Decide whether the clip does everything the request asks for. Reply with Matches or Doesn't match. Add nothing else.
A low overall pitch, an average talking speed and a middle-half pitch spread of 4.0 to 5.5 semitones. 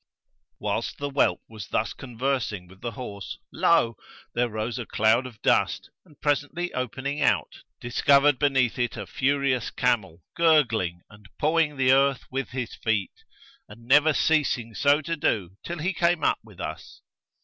Matches